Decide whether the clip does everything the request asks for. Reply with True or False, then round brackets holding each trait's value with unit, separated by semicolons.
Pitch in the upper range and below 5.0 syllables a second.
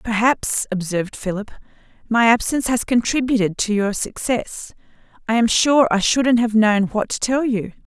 True (225 Hz; 4.8 syllables/s)